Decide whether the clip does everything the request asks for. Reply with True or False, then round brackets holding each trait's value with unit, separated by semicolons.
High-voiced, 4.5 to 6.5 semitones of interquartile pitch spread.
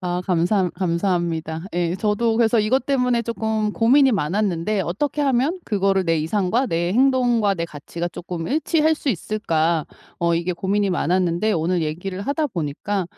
True (195 Hz; 5.3 semitones)